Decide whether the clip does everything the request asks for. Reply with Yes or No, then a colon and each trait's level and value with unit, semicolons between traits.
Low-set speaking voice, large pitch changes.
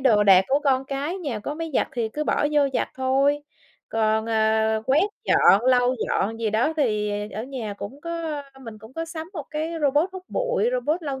No: very high, 265 Hz; wide, 5.7 semitones